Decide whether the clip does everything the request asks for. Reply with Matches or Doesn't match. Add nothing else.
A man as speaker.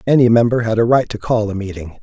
Matches